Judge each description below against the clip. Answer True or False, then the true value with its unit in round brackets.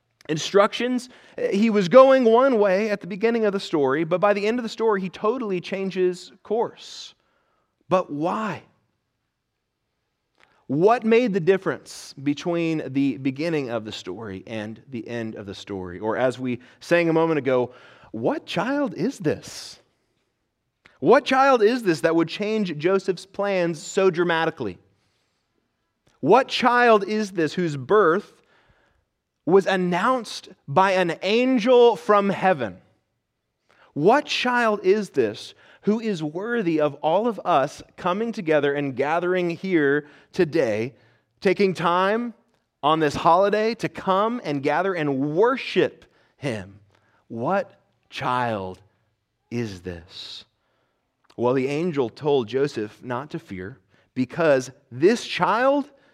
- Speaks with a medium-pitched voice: True (170 Hz)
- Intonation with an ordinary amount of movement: False (8.1 semitones)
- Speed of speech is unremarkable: False (130 wpm)